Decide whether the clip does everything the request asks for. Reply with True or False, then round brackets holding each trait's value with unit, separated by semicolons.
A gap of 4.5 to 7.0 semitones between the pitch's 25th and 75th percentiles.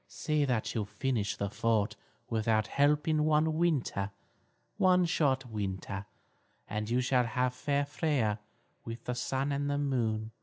True (4.9 semitones)